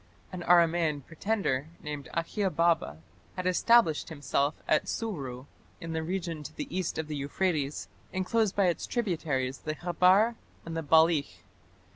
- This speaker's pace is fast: No, average, 140 wpm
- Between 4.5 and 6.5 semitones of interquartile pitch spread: No, average, 3.8 semitones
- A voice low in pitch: No, medium, 165 Hz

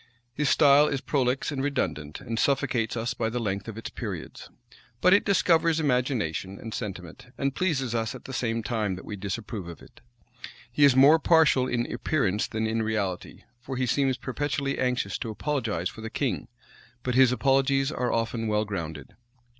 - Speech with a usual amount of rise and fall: Yes, average, 4.1 semitones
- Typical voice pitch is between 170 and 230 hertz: No, low, 125 Hz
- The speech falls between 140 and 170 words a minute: No, average, 180 wpm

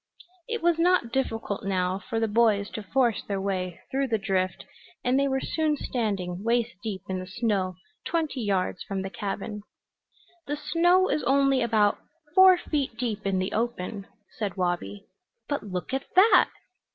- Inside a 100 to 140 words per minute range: No, average, 165 wpm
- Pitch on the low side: No, high, 225 Hz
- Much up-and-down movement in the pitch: Yes, wide, 5.8 semitones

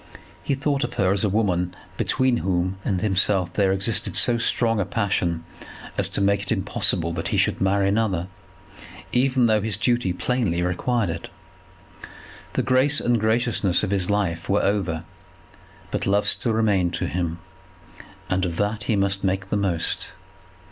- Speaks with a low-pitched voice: Yes, low, 100 Hz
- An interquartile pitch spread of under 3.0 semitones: No, average, 3.5 semitones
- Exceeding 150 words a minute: Yes, average, 165 wpm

